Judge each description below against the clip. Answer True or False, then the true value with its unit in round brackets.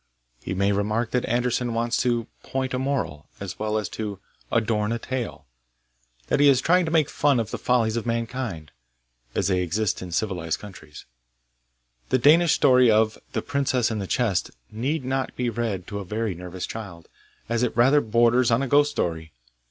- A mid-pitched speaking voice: False (115 Hz)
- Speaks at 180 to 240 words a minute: True (190 wpm)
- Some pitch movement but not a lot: True (4.4 semitones)